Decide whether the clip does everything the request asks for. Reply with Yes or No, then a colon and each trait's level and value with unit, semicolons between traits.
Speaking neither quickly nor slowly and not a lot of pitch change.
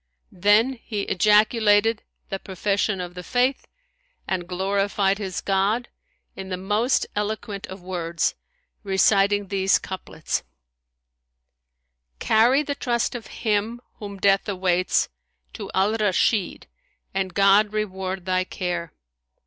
No: slow, 115 wpm; narrow, 2.2 semitones